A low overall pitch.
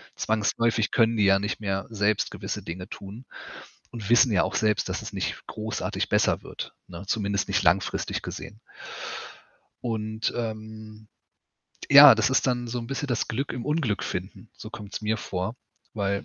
Yes: low, 110 Hz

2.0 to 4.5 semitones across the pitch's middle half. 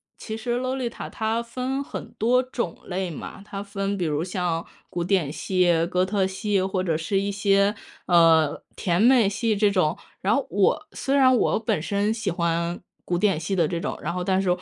Yes: average, 3.9 semitones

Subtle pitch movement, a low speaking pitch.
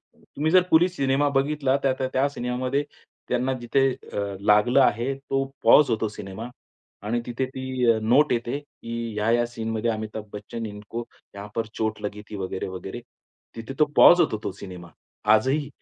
No: average, 3.7 semitones; low, 120 Hz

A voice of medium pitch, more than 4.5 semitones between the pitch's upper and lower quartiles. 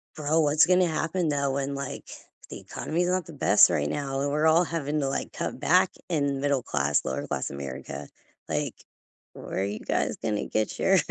Yes: medium, 145 Hz; average, 5.2 semitones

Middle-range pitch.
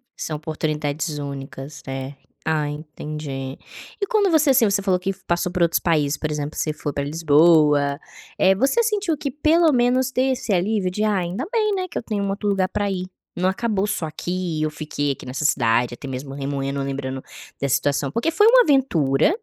Yes: medium, 165 Hz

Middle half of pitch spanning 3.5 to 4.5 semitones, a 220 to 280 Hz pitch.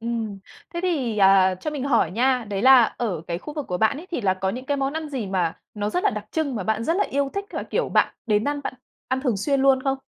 No: wide, 5.6 semitones; very high, 250 Hz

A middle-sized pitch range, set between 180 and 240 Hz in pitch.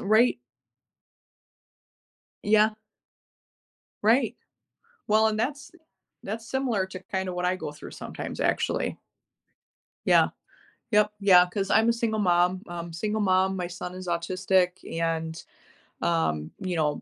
Yes: average, 3.6 semitones; high, 190 Hz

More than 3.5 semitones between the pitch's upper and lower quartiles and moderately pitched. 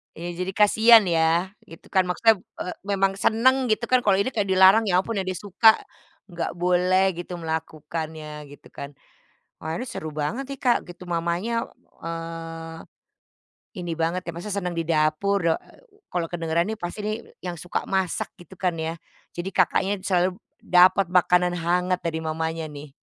No: average, 3.2 semitones; medium, 180 Hz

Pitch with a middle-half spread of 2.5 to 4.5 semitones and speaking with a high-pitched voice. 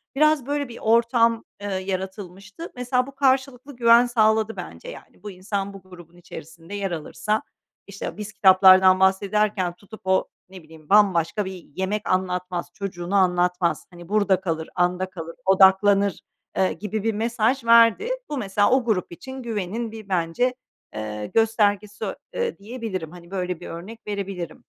Yes: average, 3.8 semitones; high, 200 Hz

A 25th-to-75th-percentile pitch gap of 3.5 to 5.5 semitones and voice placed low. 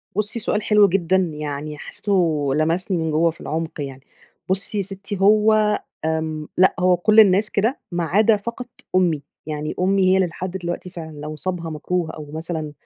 No: average, 4.0 semitones; medium, 175 Hz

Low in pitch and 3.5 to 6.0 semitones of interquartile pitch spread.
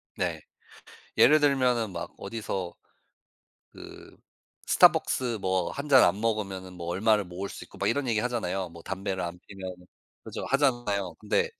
Yes: low, 100 Hz; average, 4.8 semitones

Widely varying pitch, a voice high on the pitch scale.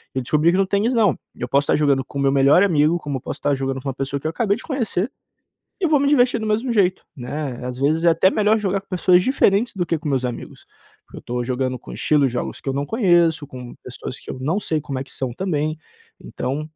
No: wide, 6.6 semitones; medium, 155 Hz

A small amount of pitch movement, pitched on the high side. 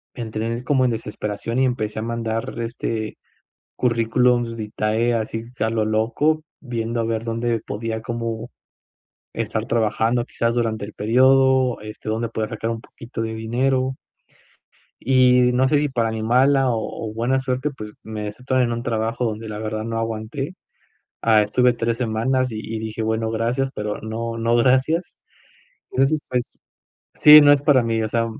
No: narrow, 2.3 semitones; low, 115 Hz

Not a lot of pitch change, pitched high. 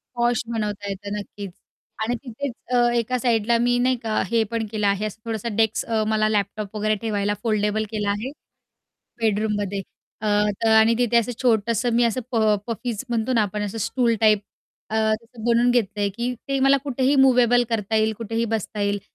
Yes: narrow, 2.2 semitones; high, 220 Hz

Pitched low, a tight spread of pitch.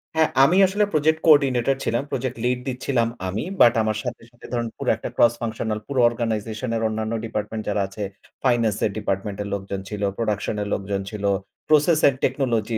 No: low, 115 Hz; average, 3.4 semitones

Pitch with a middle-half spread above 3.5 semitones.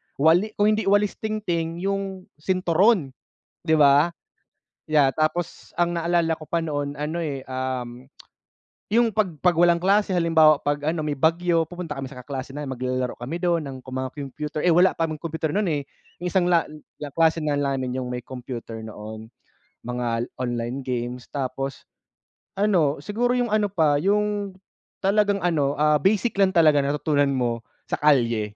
Yes: average, 5.0 semitones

